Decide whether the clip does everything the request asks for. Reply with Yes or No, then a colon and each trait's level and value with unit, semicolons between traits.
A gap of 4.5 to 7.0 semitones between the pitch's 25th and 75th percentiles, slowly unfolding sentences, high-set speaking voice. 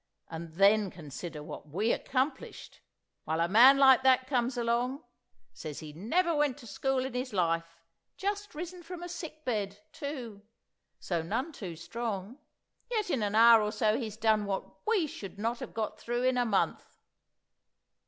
No: wide, 5.6 semitones; average, 165 wpm; high, 235 Hz